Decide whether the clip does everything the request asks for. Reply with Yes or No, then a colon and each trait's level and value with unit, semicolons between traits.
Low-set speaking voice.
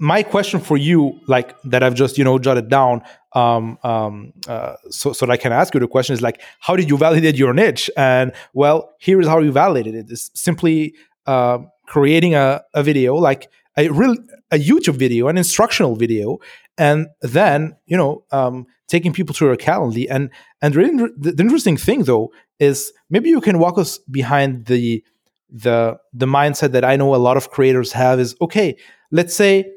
No: medium, 145 Hz